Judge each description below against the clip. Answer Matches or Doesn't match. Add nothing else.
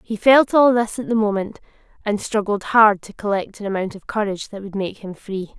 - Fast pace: Matches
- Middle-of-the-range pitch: Doesn't match